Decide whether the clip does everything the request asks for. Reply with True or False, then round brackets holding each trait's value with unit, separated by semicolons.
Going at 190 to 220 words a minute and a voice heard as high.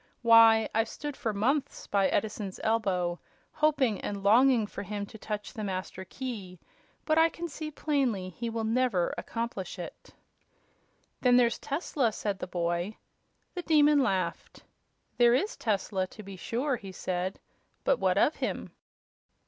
False (150 wpm; 220 Hz)